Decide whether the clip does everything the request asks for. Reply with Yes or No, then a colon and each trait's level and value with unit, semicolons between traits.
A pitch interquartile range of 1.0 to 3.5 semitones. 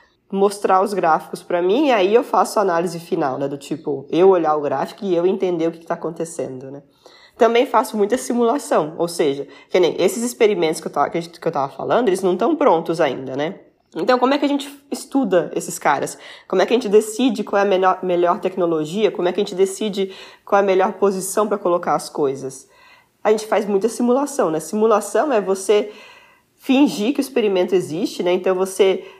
No: average, 4.5 semitones